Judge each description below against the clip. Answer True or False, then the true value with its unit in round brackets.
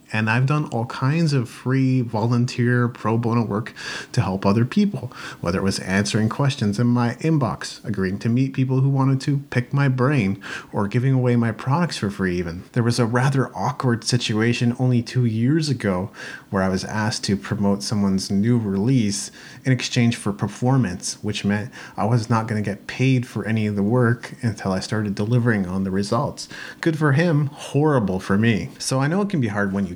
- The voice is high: False (120 Hz)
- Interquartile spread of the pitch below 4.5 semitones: True (4.1 semitones)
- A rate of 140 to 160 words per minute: False (200 wpm)